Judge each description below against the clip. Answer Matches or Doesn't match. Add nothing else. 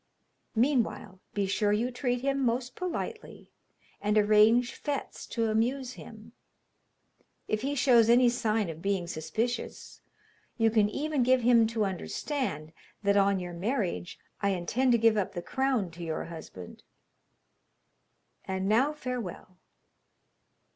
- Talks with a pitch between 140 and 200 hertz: Doesn't match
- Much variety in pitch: Doesn't match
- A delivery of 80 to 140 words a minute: Matches